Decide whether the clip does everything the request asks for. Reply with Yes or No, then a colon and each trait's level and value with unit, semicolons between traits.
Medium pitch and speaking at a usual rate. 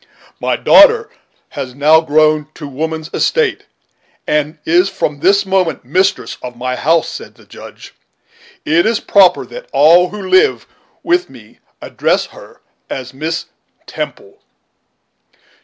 No: medium, 165 Hz; slow, 130 wpm